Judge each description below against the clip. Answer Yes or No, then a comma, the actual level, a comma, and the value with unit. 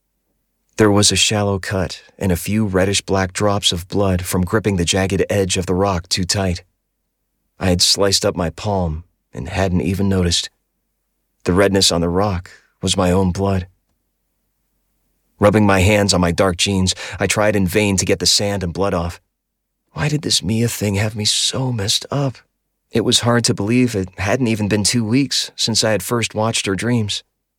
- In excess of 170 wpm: Yes, average, 190 wpm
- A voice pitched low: Yes, low, 100 Hz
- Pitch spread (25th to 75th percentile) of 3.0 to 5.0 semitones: No, narrow, 2.5 semitones